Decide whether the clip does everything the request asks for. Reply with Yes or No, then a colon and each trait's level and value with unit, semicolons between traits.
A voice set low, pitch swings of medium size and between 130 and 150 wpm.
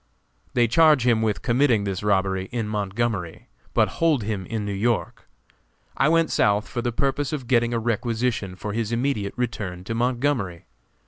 No: low, 115 Hz; average, 3.5 semitones; average, 170 wpm